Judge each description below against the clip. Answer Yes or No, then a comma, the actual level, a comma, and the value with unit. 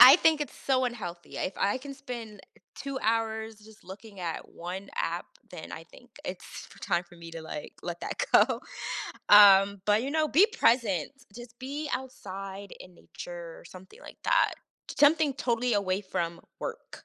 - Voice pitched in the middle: No, high, 215 Hz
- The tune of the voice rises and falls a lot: Yes, wide, 5.8 semitones